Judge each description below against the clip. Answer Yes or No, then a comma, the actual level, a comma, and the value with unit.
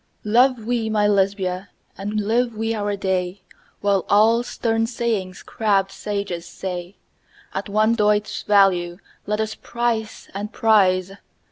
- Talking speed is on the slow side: Yes, slow, 130 wpm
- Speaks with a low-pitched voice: No, high, 210 Hz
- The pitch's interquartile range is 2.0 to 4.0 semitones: Yes, narrow, 2.5 semitones